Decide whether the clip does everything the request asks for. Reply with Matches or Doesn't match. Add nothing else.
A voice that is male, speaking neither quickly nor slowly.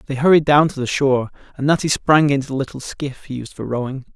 Doesn't match